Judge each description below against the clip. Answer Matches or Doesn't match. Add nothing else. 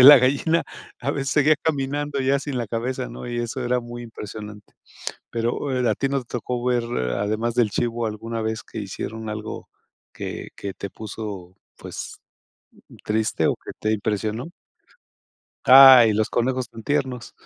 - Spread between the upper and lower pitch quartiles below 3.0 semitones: Doesn't match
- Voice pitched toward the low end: Matches